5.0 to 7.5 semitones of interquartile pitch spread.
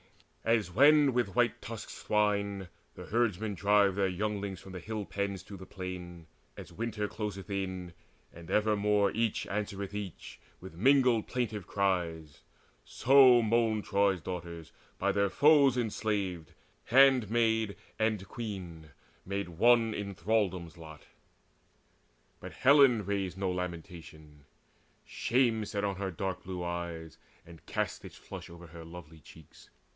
No: average, 3.8 semitones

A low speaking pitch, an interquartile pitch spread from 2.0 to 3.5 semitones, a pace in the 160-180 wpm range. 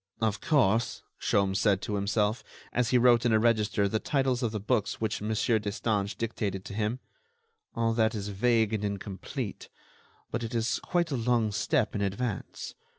Yes: low, 110 Hz; narrow, 2.6 semitones; average, 175 wpm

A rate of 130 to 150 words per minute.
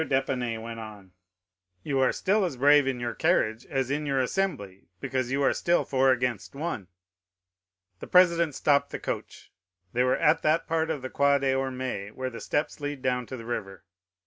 No: average, 185 wpm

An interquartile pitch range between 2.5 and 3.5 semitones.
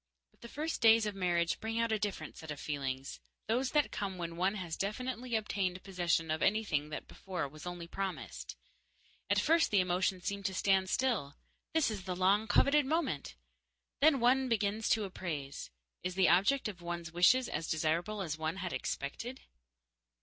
No: average, 4.8 semitones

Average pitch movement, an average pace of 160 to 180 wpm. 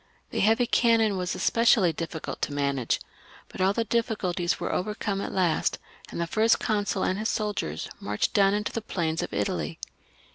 Yes: average, 4.7 semitones; average, 175 wpm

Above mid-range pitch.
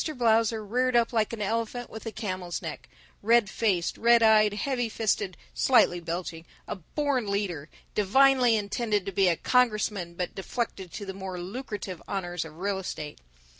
Yes: high, 210 Hz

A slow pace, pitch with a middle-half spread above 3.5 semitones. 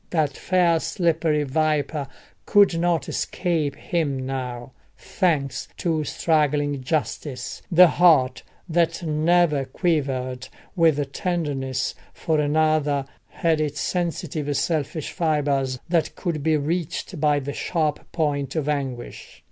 No: slow, 115 wpm; average, 3.0 semitones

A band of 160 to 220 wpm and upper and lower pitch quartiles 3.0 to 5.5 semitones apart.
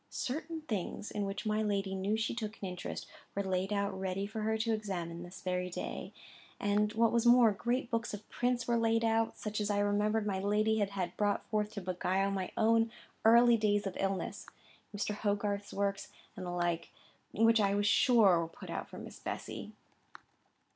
No: average, 190 wpm; narrow, 2.4 semitones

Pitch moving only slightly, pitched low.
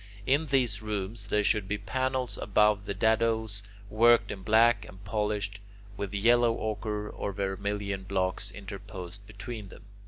Yes: narrow, 2.0 semitones; low, 105 Hz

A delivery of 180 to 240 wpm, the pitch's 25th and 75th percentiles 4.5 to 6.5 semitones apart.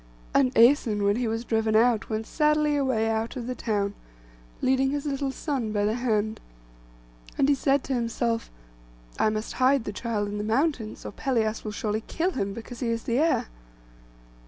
No: average, 185 wpm; average, 3.6 semitones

